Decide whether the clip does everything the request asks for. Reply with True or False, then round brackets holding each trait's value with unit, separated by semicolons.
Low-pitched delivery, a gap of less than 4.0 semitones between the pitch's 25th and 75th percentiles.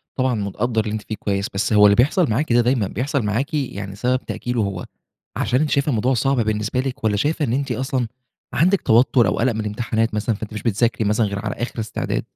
True (115 Hz; 3.6 semitones)